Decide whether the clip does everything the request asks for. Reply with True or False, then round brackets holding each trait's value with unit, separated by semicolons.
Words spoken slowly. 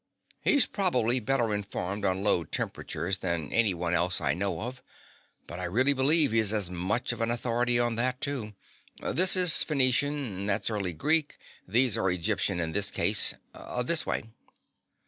False (165 wpm)